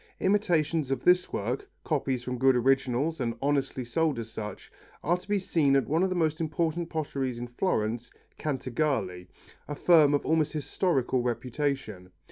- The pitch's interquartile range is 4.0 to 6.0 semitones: Yes, average, 4.7 semitones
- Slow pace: No, average, 160 wpm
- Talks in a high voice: No, medium, 140 Hz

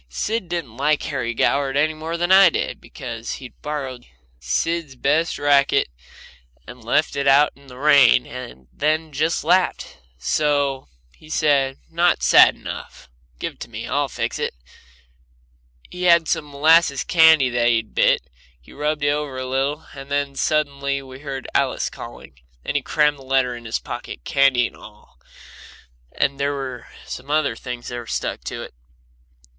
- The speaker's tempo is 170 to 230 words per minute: Yes, average, 175 wpm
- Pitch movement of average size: Yes, average, 3.1 semitones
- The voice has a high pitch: No, medium, 140 Hz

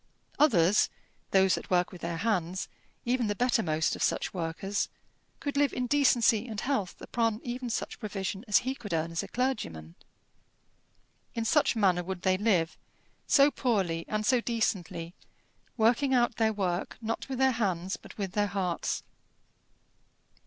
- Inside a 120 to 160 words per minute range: Yes, average, 155 wpm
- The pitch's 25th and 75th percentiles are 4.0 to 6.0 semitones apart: Yes, average, 5.0 semitones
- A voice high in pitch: Yes, high, 210 Hz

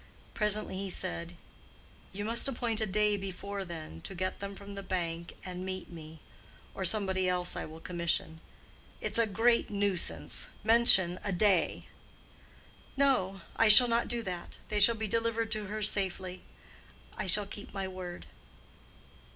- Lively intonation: No, average, 3.0 semitones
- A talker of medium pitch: No, high, 195 Hz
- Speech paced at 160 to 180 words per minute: No, average, 150 wpm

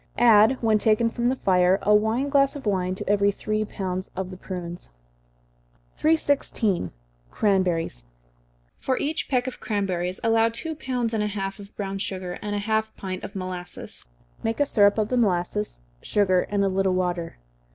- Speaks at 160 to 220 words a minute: Yes, average, 170 wpm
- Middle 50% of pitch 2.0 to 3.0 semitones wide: No, average, 3.5 semitones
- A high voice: Yes, high, 205 Hz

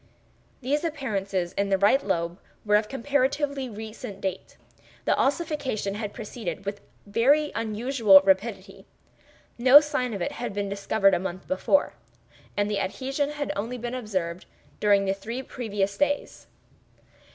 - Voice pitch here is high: Yes, high, 215 Hz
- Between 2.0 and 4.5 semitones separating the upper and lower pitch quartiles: No, average, 5.1 semitones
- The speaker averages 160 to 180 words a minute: No, average, 140 wpm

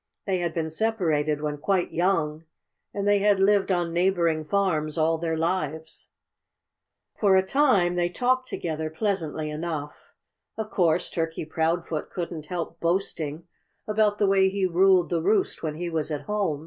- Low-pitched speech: No, medium, 175 Hz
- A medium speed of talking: Yes, average, 160 wpm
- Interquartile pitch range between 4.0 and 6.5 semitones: No, average, 3.6 semitones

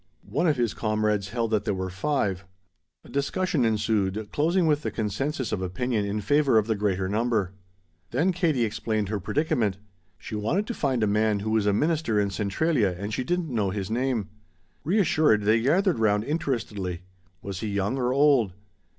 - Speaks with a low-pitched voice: Yes, low, 110 Hz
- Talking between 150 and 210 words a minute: Yes, average, 180 wpm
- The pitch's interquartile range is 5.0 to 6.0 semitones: Yes, wide, 5.6 semitones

